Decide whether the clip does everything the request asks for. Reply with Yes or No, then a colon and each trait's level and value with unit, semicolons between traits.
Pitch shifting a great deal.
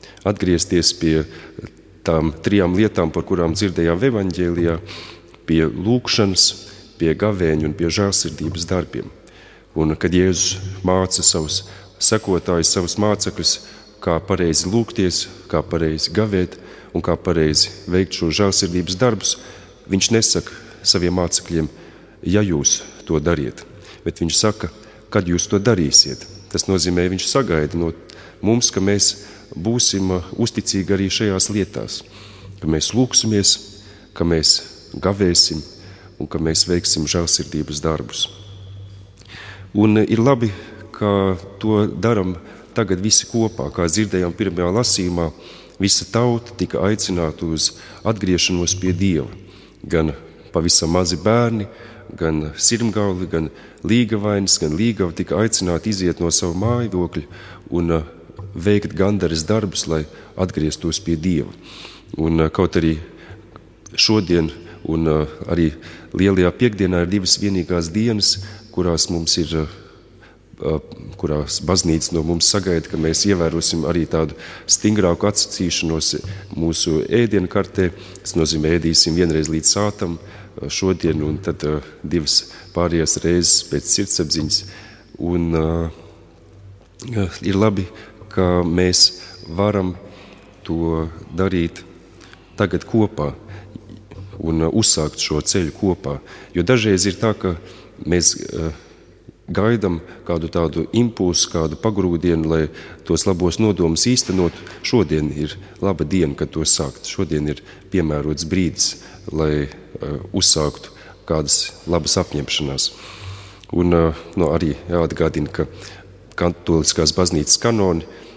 No: average, 3.5 semitones